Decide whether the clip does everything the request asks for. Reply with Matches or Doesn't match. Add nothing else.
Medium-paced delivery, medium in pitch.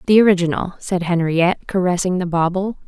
Matches